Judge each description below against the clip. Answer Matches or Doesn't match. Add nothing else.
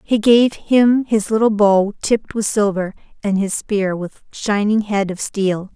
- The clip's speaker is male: Doesn't match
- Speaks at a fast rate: Doesn't match